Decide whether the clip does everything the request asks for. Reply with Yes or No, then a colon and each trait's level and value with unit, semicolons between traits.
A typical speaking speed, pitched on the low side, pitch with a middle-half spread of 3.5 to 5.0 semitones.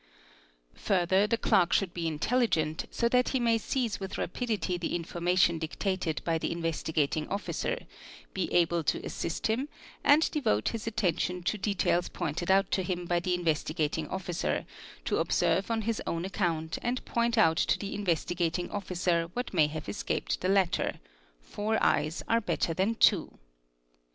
No: average, 155 wpm; medium, 180 Hz; average, 4.1 semitones